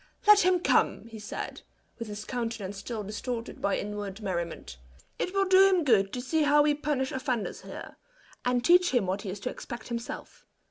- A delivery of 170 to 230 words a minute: Yes, average, 190 wpm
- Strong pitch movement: Yes, wide, 6.2 semitones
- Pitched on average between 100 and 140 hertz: No, high, 240 Hz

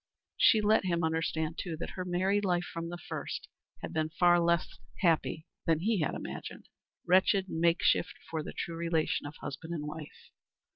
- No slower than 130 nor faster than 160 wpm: No, average, 175 wpm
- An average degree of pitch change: No, narrow, 2.1 semitones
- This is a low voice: No, medium, 170 Hz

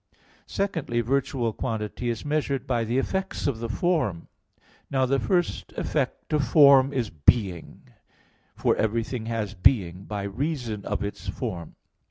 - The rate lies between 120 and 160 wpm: Yes, average, 140 wpm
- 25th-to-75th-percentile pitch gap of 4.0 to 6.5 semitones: Yes, average, 4.7 semitones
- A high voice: No, low, 120 Hz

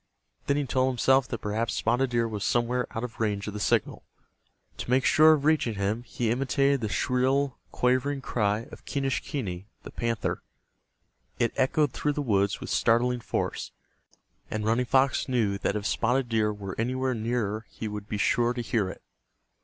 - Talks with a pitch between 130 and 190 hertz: No, low, 120 Hz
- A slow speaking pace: No, average, 175 wpm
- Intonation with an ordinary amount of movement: Yes, average, 3.5 semitones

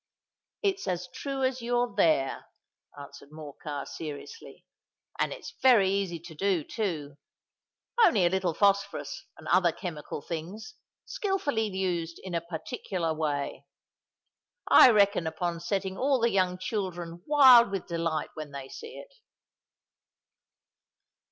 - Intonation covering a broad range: Yes, wide, 5.7 semitones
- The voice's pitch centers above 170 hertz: Yes, medium, 185 Hz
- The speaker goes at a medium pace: No, slow, 125 wpm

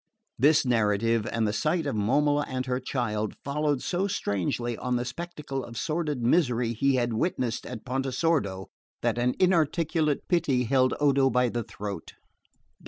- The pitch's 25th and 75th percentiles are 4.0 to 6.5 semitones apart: Yes, average, 4.3 semitones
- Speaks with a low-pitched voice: Yes, low, 130 Hz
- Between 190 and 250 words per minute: No, average, 155 wpm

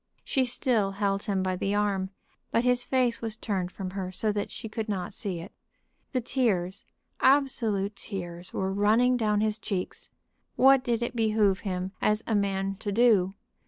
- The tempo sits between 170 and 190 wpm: Yes, average, 175 wpm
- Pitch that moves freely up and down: No, average, 3.2 semitones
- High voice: Yes, high, 205 Hz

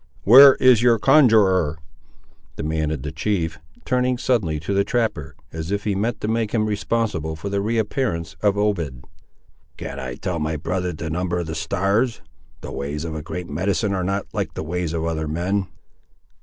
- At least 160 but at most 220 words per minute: Yes, average, 185 wpm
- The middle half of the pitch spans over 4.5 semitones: Yes, average, 5.1 semitones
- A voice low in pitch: Yes, very low, 90 Hz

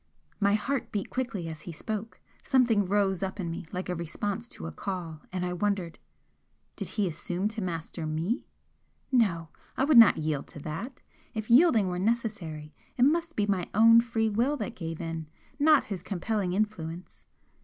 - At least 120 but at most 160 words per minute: No, average, 175 wpm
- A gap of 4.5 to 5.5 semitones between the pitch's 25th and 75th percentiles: Yes, average, 5.1 semitones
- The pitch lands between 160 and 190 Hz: No, high, 200 Hz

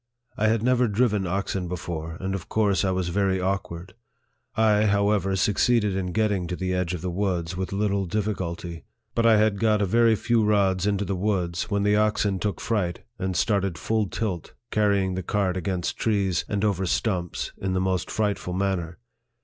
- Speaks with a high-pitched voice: No, very low, 95 Hz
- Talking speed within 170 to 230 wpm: Yes, average, 190 wpm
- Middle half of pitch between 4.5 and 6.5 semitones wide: No, narrow, 2.4 semitones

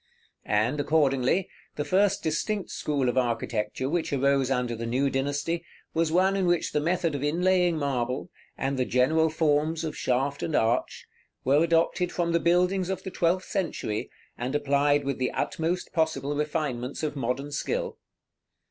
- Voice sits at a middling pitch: Yes, medium, 150 Hz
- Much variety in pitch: No, average, 4.2 semitones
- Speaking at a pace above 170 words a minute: No, average, 160 wpm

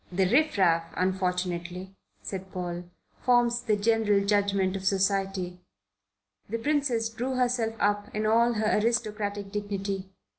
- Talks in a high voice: Yes, high, 205 Hz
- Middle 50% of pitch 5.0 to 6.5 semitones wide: No, average, 3.2 semitones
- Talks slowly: Yes, slow, 125 wpm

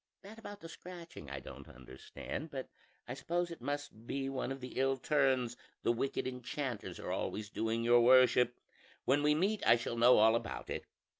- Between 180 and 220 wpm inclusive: Yes, average, 190 wpm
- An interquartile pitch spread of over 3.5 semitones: Yes, average, 4.0 semitones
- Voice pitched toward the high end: No, low, 130 Hz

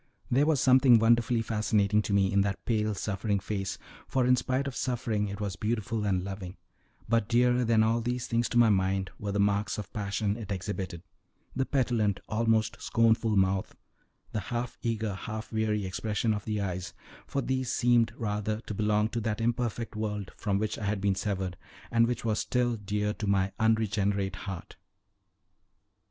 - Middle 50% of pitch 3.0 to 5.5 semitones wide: No, narrow, 2.6 semitones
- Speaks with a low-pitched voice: Yes, low, 110 Hz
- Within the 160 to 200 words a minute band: Yes, average, 180 wpm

